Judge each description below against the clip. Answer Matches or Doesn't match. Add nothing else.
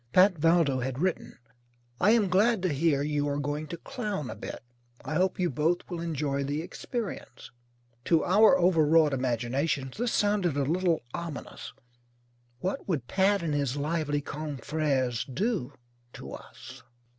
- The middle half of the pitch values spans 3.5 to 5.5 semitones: Matches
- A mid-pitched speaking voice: Matches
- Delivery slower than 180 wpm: Matches